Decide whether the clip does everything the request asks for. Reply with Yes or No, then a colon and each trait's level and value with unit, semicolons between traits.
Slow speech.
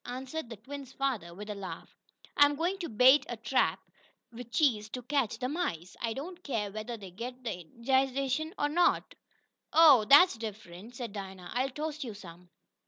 No: average, 175 wpm